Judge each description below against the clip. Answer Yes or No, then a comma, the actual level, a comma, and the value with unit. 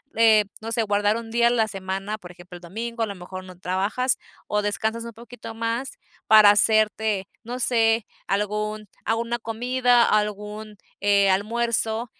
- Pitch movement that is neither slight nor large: No, narrow, 2.2 semitones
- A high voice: Yes, high, 215 Hz